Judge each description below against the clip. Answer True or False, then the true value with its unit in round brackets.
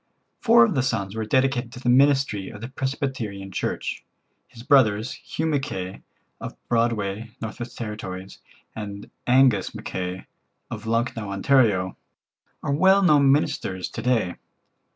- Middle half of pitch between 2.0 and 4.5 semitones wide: False (4.9 semitones)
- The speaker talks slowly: True (130 wpm)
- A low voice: True (115 Hz)